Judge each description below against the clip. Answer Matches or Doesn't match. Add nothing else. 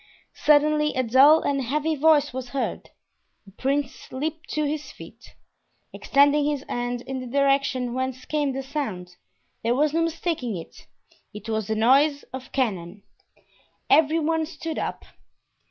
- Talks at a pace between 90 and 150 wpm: Matches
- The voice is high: Matches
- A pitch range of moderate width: Matches